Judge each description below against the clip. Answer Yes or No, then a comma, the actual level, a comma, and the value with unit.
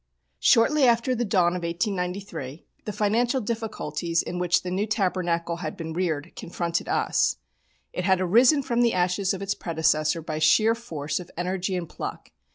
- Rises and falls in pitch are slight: No, average, 4.2 semitones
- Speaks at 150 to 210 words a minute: Yes, average, 165 wpm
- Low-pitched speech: No, medium, 180 Hz